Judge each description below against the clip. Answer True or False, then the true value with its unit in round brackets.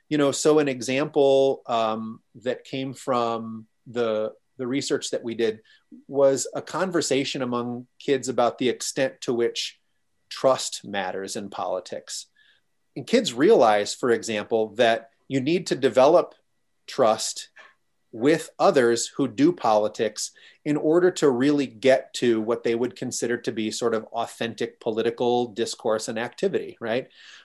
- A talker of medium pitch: False (120 Hz)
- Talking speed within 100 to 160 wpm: True (140 wpm)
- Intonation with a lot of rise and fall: False (3.2 semitones)